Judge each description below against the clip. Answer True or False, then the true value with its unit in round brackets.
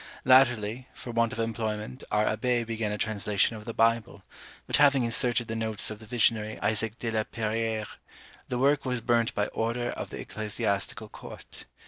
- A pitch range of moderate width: False (1.9 semitones)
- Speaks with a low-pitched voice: True (115 Hz)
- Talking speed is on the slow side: False (180 wpm)